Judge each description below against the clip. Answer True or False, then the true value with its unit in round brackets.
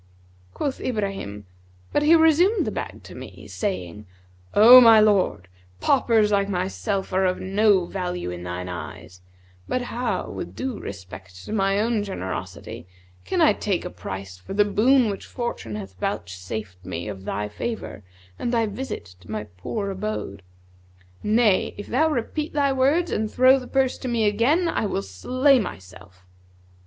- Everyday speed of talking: True (160 wpm)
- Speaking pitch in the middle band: False (200 Hz)